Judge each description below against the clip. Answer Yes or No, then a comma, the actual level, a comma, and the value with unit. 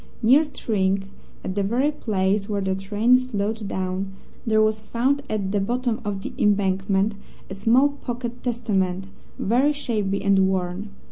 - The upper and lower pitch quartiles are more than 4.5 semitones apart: No, average, 3.8 semitones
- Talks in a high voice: Yes, high, 210 Hz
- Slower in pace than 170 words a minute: Yes, average, 150 wpm